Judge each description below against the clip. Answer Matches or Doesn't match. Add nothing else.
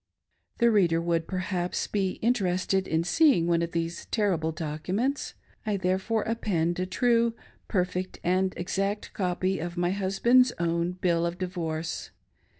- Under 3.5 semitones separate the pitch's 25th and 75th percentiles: Matches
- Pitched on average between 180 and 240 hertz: Matches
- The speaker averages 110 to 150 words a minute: Matches